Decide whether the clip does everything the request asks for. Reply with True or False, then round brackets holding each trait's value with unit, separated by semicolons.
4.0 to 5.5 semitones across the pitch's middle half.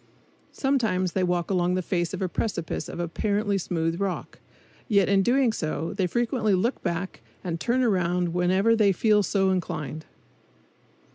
False (3.3 semitones)